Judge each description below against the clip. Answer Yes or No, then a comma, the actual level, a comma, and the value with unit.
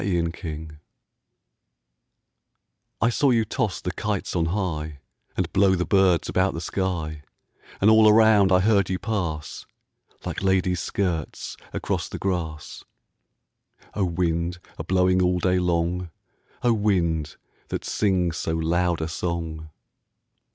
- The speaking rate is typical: No, slow, 115 wpm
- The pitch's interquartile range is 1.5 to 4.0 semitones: Yes, average, 3.0 semitones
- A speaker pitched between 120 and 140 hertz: No, very low, 90 Hz